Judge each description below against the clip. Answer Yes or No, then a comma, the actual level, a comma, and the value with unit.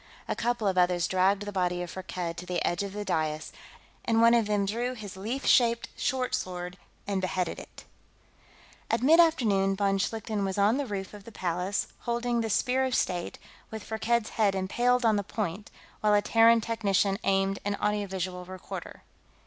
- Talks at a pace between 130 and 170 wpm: No, average, 190 wpm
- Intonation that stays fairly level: No, average, 3.5 semitones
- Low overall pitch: No, high, 205 Hz